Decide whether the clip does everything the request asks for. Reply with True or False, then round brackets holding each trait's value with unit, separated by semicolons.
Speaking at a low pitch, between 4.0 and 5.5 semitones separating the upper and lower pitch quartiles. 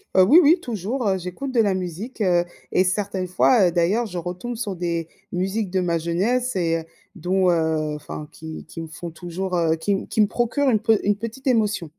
False (190 Hz; 4.5 semitones)